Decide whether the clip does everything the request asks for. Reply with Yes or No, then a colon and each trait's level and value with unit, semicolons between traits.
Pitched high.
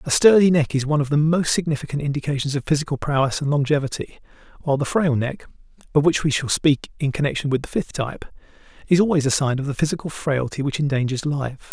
No: medium, 145 Hz